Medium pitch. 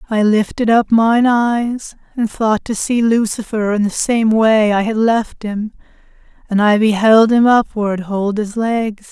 No: high, 220 Hz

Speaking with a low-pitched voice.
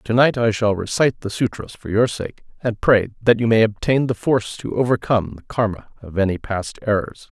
Yes: low, 110 Hz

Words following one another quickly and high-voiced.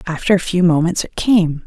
No: fast, 215 wpm; medium, 175 Hz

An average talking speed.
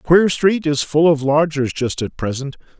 Yes: average, 195 wpm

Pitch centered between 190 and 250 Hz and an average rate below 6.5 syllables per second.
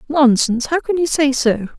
No: very high, 275 Hz; 5.2 syllables/s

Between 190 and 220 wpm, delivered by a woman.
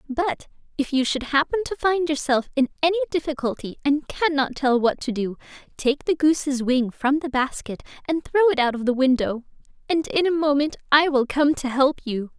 Yes: average, 200 wpm; female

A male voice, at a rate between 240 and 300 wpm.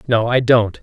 No: male; fast, 220 wpm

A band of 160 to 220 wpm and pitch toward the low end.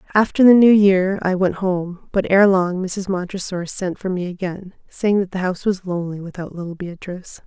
No: average, 200 wpm; medium, 185 Hz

